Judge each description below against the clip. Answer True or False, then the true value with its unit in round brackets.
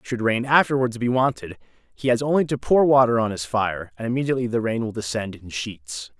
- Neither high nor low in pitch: False (115 Hz)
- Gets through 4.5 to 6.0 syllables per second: True (5.7 syllables/s)